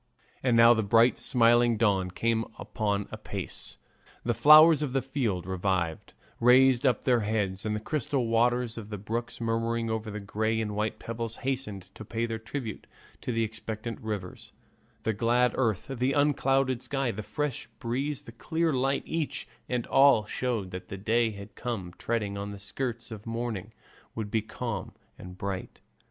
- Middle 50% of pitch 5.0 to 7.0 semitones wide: No, average, 2.9 semitones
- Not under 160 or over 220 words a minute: Yes, average, 170 wpm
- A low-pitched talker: Yes, low, 115 Hz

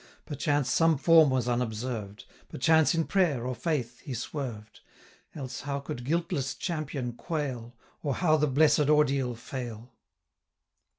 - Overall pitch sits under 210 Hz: Yes, low, 135 Hz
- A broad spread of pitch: No, average, 3.9 semitones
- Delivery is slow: Yes, slow, 130 wpm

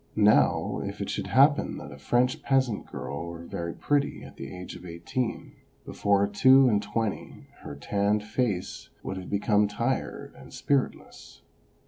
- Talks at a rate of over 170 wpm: No, average, 155 wpm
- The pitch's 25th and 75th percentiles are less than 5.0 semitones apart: No, wide, 5.6 semitones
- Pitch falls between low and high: No, low, 105 Hz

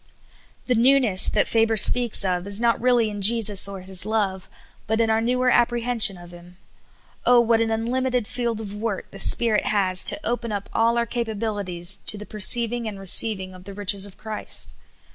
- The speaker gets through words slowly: No, average, 195 wpm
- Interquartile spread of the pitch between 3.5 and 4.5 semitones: No, average, 3.1 semitones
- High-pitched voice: Yes, high, 220 Hz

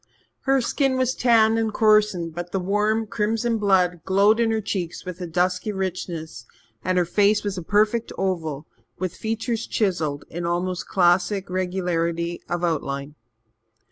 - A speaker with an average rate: Yes, average, 150 wpm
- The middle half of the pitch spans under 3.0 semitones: No, average, 3.7 semitones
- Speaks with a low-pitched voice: No, medium, 185 Hz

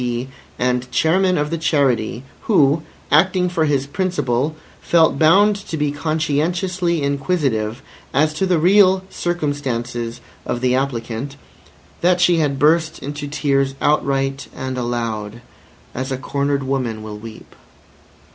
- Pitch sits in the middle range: Yes, medium, 145 Hz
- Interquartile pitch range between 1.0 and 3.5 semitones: No, average, 4.5 semitones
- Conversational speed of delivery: No, slow, 130 wpm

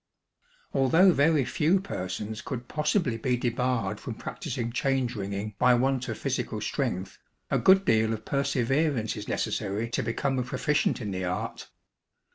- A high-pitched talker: No, low, 125 Hz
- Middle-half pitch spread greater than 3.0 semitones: Yes, average, 4.3 semitones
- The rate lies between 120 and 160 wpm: Yes, average, 150 wpm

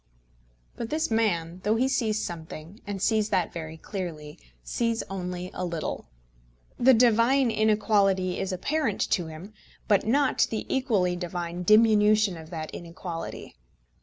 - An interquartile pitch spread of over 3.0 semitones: Yes, average, 4.4 semitones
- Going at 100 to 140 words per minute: Yes, slow, 135 wpm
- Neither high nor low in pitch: No, high, 195 Hz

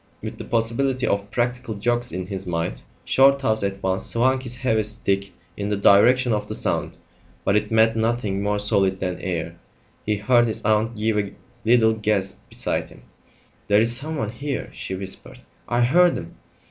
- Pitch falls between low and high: No, low, 110 Hz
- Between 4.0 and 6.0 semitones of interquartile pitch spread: No, average, 3.3 semitones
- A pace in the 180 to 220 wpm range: No, average, 170 wpm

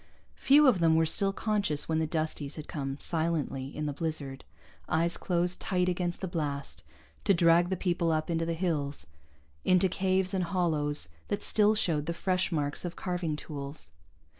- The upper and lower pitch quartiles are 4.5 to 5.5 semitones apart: No, average, 3.3 semitones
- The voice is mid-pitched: Yes, medium, 165 Hz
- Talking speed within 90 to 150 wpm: No, average, 175 wpm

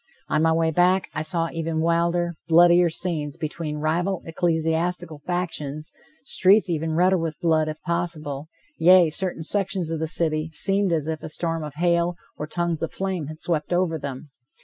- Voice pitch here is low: No, medium, 165 Hz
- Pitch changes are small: Yes, narrow, 2.0 semitones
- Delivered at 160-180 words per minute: Yes, average, 170 wpm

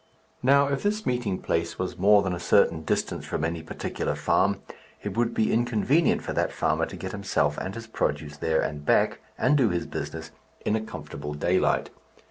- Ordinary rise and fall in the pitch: No, wide, 6.7 semitones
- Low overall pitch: Yes, very low, 95 Hz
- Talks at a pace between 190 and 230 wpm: Yes, average, 195 wpm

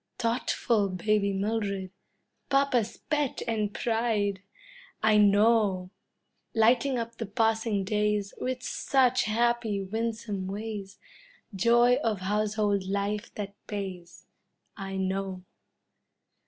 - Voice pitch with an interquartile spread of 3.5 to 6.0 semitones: No, average, 2.7 semitones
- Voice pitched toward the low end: No, high, 210 Hz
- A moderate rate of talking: No, slow, 100 wpm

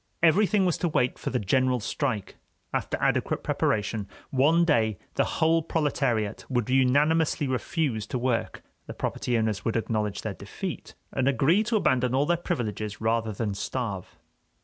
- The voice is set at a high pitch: No, low, 125 Hz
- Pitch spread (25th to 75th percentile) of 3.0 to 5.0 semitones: No, wide, 5.5 semitones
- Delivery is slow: No, average, 155 wpm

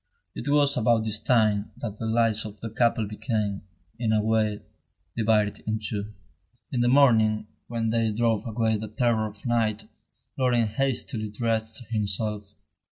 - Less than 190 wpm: Yes, average, 155 wpm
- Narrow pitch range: Yes, narrow, 1.6 semitones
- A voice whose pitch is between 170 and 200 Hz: No, low, 110 Hz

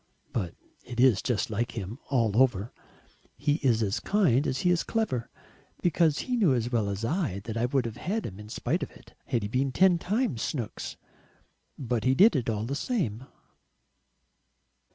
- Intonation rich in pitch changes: Yes, wide, 6.1 semitones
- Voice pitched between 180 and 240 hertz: No, low, 125 Hz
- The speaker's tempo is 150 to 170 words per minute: No, average, 190 wpm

